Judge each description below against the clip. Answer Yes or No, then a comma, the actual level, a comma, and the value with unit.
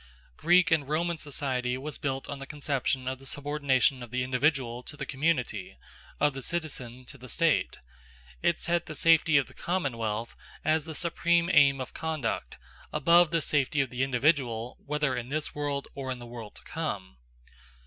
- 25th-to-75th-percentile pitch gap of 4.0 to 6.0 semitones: No, average, 3.6 semitones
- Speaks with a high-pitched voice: No, medium, 140 Hz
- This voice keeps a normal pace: Yes, average, 180 wpm